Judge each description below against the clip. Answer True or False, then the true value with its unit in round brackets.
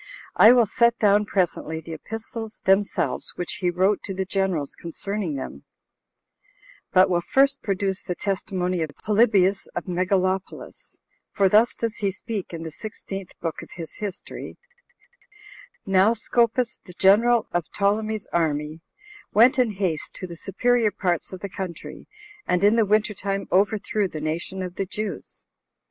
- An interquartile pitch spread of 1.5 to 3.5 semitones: True (3.2 semitones)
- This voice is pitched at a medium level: False (195 Hz)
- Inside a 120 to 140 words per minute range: False (155 wpm)